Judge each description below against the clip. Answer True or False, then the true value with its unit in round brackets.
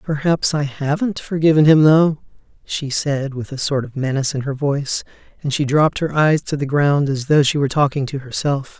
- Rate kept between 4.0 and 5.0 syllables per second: False (5.3 syllables/s)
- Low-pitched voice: False (145 Hz)